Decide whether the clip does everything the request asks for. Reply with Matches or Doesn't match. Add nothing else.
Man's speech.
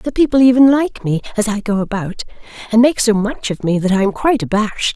Doesn't match